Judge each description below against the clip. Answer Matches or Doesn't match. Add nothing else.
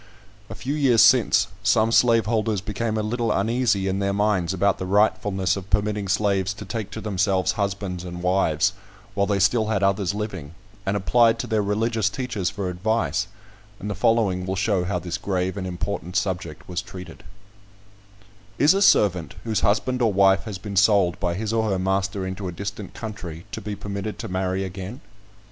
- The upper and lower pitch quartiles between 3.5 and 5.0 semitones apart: Doesn't match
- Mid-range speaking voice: Doesn't match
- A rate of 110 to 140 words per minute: Doesn't match